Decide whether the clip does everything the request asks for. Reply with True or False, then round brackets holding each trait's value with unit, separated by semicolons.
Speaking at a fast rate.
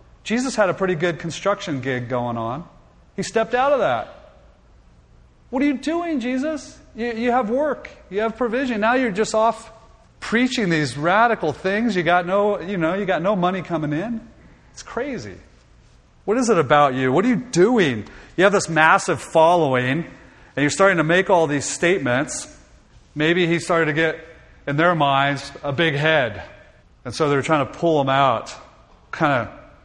False (180 wpm)